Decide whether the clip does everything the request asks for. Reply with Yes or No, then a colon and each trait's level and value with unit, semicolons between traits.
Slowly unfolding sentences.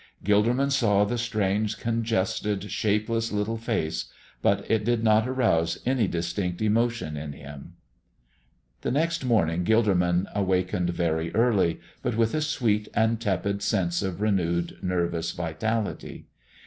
Yes: slow, 130 wpm